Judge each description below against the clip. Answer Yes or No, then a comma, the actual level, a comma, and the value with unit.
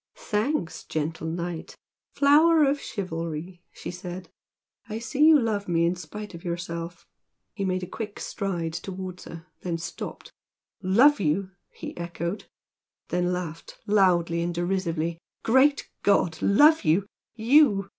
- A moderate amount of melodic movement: Yes, average, 4.0 semitones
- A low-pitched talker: No, medium, 180 Hz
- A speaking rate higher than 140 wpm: No, slow, 135 wpm